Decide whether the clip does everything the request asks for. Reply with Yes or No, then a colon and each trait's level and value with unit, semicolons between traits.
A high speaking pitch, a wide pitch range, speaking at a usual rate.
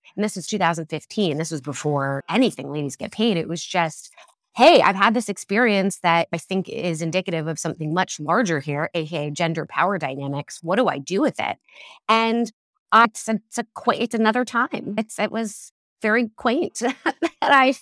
Yes: high, 195 Hz; wide, 5.8 semitones; average, 180 wpm